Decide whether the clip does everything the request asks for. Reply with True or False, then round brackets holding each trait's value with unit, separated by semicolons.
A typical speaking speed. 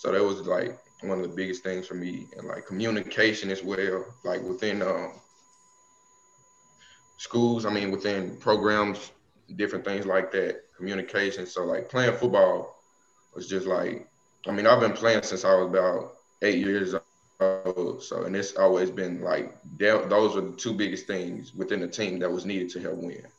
True (175 wpm)